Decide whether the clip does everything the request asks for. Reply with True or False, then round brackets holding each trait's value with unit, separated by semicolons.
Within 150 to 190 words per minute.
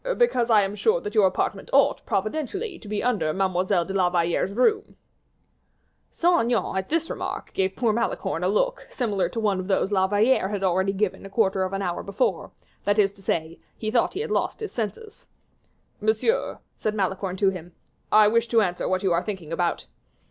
False (200 wpm)